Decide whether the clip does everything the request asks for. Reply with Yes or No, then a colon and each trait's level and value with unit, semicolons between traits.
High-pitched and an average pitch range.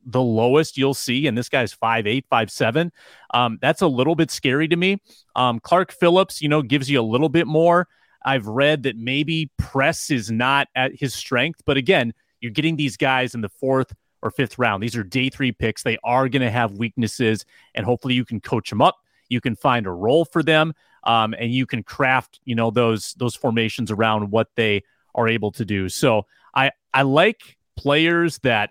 No: low, 130 Hz; average, 4.2 semitones